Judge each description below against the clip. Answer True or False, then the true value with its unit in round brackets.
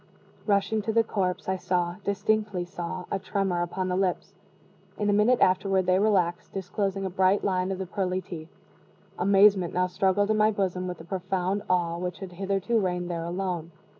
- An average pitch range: False (1.9 semitones)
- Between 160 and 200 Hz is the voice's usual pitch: True (190 Hz)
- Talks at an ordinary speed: True (185 wpm)